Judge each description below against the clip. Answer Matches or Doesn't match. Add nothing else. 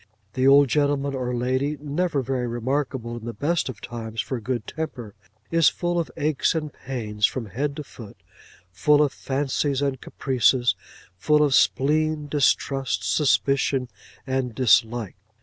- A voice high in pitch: Doesn't match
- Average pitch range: Matches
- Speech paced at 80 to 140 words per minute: Doesn't match